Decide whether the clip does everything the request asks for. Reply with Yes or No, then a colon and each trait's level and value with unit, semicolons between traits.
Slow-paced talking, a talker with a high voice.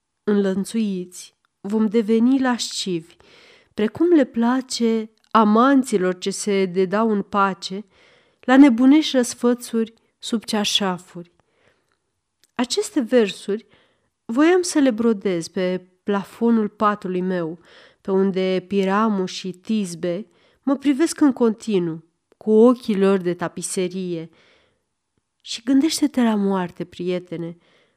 Yes: slow, 100 wpm; high, 215 Hz